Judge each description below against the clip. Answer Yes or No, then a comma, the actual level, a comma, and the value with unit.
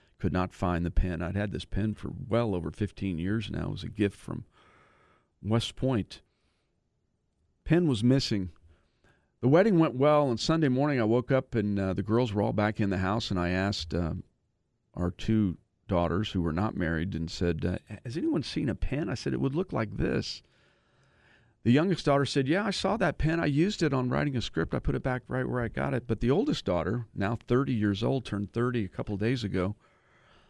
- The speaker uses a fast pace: Yes, fast, 220 wpm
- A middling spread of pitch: No, wide, 5.8 semitones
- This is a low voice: Yes, low, 105 Hz